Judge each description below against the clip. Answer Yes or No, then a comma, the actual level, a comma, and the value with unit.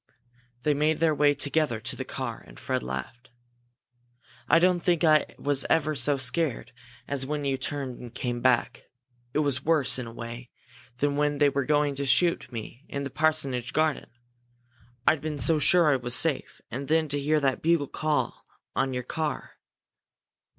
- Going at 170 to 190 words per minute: Yes, average, 180 wpm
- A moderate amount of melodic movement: Yes, average, 3.2 semitones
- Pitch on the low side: No, medium, 145 Hz